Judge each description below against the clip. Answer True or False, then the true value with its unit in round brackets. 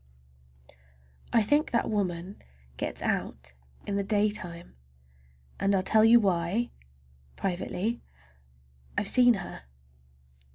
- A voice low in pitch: False (185 Hz)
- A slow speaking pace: True (90 wpm)